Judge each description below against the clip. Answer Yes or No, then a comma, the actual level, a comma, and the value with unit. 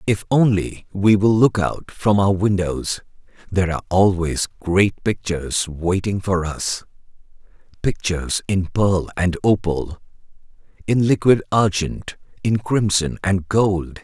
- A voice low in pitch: Yes, very low, 95 Hz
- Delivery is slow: Yes, slow, 120 wpm